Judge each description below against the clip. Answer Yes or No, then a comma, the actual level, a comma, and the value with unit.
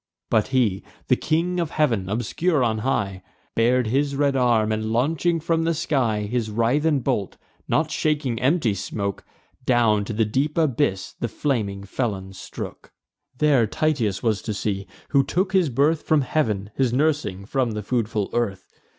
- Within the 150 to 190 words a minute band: Yes, average, 160 wpm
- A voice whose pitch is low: Yes, low, 120 Hz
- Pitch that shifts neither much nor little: No, wide, 5.8 semitones